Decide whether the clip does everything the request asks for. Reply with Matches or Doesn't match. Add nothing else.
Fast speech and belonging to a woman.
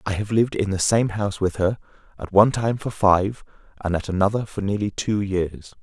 Doesn't match